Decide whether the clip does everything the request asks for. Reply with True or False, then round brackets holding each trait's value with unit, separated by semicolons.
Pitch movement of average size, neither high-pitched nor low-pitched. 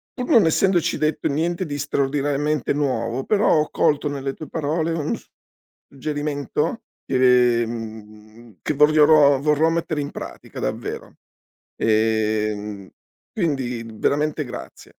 True (4.6 semitones; 145 Hz)